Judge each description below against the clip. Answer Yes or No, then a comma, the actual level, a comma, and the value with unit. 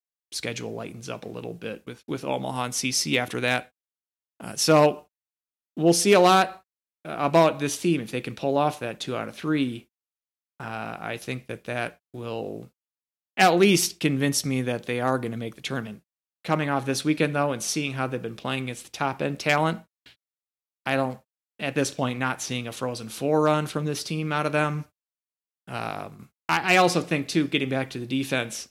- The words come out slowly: No, average, 195 wpm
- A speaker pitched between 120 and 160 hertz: Yes, low, 135 Hz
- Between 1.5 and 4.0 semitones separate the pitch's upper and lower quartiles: No, average, 4.4 semitones